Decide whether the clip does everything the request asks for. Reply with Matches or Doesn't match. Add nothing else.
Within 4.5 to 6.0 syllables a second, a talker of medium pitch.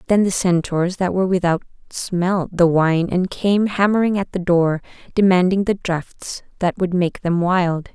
Doesn't match